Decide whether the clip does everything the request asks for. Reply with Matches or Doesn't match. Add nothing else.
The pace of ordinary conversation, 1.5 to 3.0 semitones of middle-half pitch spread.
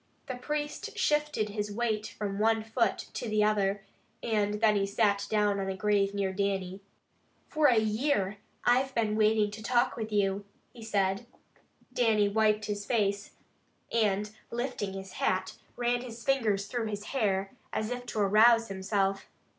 Matches